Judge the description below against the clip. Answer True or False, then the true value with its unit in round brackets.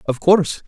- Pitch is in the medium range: True (170 Hz)